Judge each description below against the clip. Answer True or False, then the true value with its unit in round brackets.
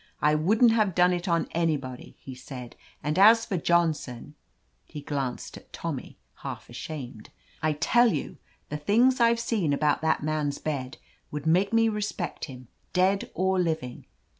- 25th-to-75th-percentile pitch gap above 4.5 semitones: True (5.4 semitones)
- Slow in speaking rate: False (170 wpm)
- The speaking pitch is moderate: True (160 Hz)